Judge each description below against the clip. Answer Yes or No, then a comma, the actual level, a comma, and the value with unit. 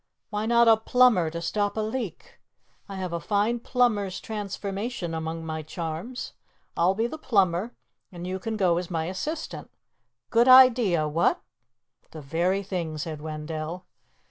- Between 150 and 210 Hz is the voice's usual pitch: Yes, high, 190 Hz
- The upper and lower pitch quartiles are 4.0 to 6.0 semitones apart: Yes, average, 5.1 semitones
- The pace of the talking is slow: No, average, 150 wpm